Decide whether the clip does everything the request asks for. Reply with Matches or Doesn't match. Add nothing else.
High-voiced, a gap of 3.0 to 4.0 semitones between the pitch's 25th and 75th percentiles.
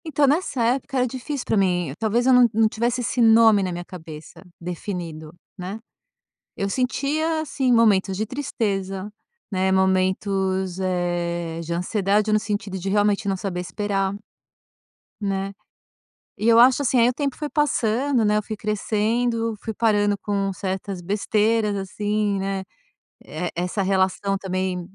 Matches